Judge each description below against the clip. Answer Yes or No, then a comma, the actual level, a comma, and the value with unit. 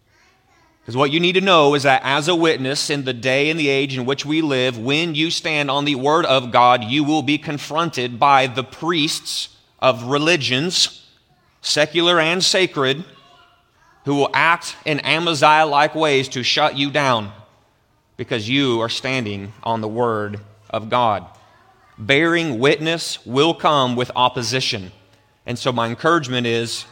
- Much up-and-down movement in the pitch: No, average, 4.1 semitones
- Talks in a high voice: No, medium, 140 Hz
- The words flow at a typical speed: Yes, average, 160 wpm